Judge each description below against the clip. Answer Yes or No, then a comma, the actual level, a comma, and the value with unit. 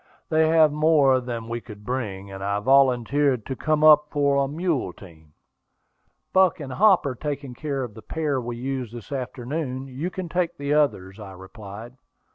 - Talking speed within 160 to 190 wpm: Yes, average, 180 wpm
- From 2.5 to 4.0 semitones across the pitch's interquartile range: No, average, 4.6 semitones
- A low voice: Yes, low, 130 Hz